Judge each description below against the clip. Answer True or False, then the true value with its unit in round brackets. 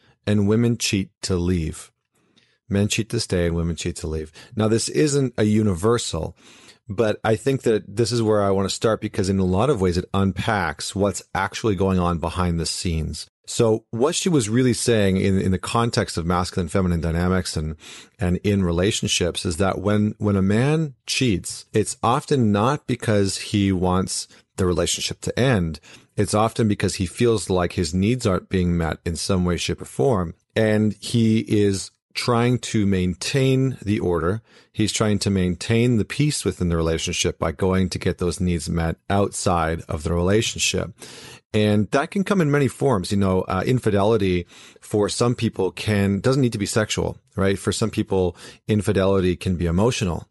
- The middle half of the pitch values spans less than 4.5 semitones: True (3.9 semitones)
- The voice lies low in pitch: True (100 Hz)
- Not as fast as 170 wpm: False (185 wpm)